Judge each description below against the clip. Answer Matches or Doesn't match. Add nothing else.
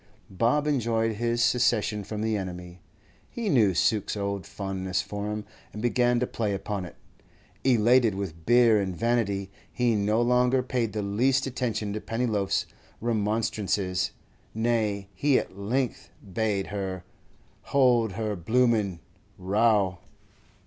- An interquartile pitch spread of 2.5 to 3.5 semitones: Matches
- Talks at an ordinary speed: Doesn't match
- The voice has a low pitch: Matches